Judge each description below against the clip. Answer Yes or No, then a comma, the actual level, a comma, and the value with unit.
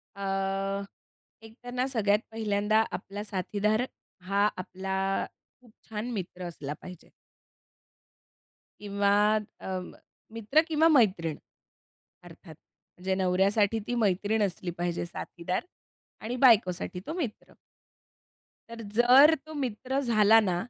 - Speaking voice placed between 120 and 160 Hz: No, high, 205 Hz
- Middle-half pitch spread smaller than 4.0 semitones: Yes, average, 3.5 semitones